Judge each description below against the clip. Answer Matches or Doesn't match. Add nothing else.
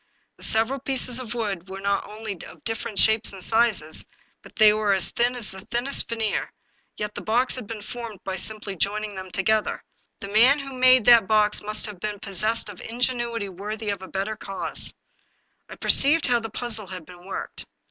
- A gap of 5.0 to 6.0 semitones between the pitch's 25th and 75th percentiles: Doesn't match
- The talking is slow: Doesn't match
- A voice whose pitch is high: Matches